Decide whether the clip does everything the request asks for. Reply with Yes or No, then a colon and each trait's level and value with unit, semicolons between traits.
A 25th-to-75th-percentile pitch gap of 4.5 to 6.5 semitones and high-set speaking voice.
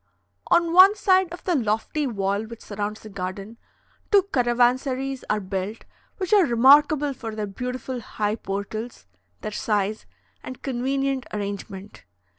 Yes: average, 4.8 semitones; high, 240 Hz